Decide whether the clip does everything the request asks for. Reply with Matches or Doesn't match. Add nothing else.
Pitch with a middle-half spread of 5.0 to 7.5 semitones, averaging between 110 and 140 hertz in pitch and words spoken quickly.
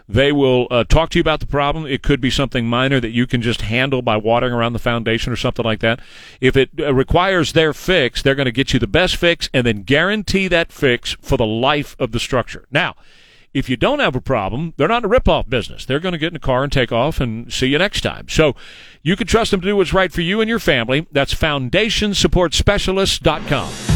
Matches